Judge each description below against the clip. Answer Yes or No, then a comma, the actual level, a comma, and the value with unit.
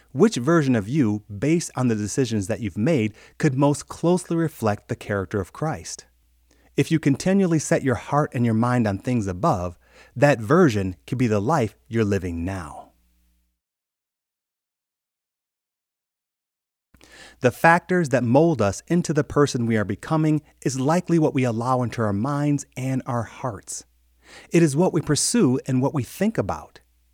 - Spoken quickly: No, average, 160 wpm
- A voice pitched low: Yes, low, 125 Hz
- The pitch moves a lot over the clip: Yes, wide, 6.9 semitones